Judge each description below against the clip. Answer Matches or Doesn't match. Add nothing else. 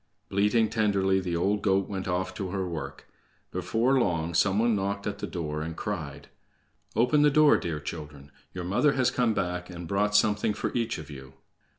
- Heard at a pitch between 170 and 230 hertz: Doesn't match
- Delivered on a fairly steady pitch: Doesn't match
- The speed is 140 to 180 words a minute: Doesn't match